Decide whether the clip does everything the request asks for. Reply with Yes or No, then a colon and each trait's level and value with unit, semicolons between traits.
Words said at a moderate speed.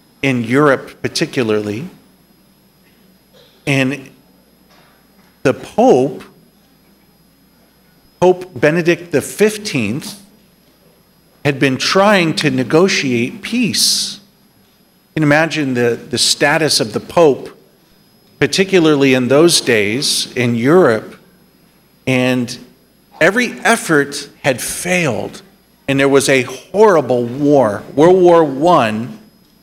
No: slow, 90 wpm